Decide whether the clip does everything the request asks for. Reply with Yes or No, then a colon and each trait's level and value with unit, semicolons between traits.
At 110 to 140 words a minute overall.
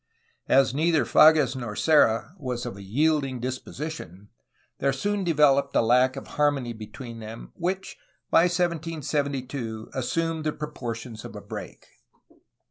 Yes: slow, 135 wpm